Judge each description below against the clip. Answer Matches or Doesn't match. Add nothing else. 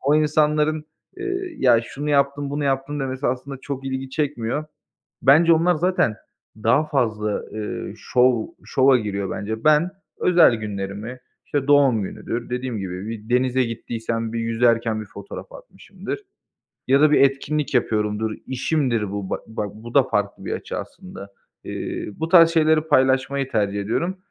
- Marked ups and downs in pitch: Doesn't match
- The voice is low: Matches